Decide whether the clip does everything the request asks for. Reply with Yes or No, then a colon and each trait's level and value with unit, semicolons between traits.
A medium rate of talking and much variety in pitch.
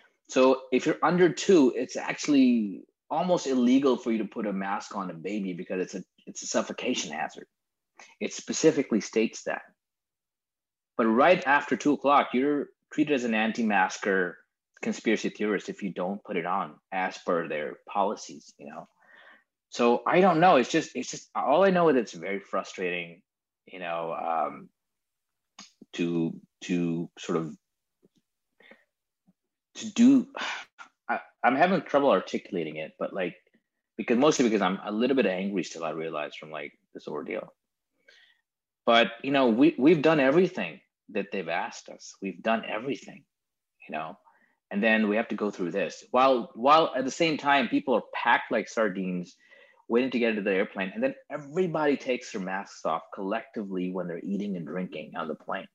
Yes: average, 170 wpm; wide, 8.6 semitones